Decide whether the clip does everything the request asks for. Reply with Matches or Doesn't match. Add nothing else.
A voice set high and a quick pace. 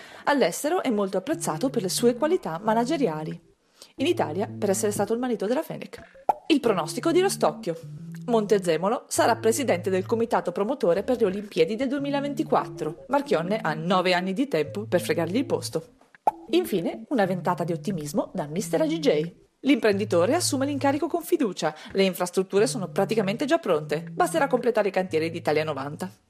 Doesn't match